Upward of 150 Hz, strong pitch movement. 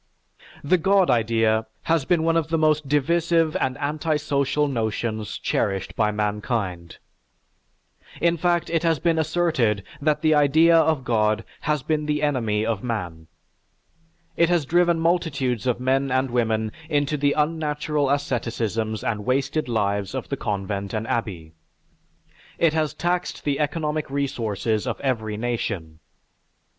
No: low, 135 Hz; wide, 6.1 semitones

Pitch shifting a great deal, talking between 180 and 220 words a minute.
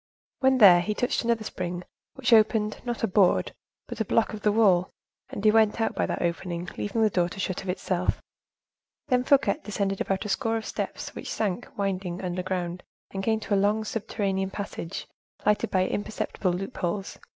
No: average, 3.1 semitones; average, 185 wpm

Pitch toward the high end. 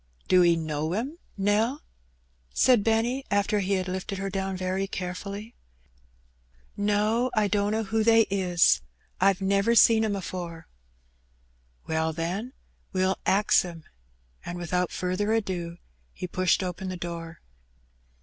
Yes: high, 195 Hz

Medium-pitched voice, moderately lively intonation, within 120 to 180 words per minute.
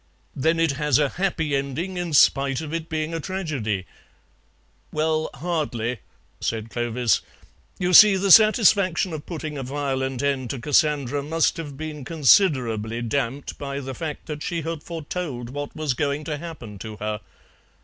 Yes: medium, 145 Hz; average, 3.9 semitones; average, 160 wpm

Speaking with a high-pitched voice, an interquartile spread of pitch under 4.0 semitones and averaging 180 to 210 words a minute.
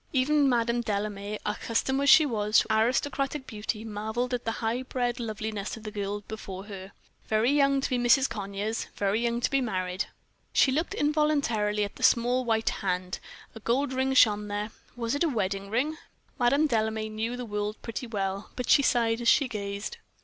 Yes: high, 225 Hz; average, 3.6 semitones; average, 185 wpm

